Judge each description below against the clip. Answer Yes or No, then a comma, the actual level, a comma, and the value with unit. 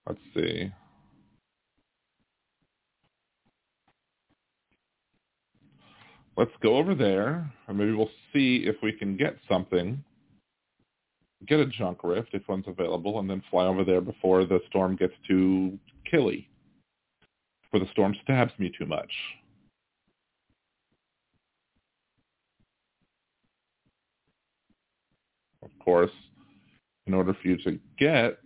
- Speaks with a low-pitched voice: Yes, very low, 95 Hz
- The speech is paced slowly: Yes, slow, 100 wpm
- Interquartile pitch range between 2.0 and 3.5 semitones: Yes, average, 2.9 semitones